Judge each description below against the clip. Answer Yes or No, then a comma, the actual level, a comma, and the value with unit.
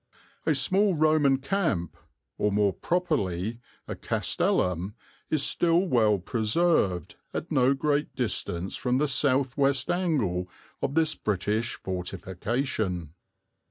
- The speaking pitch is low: Yes, low, 130 Hz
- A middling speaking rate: No, slow, 115 wpm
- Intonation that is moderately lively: No, wide, 7.7 semitones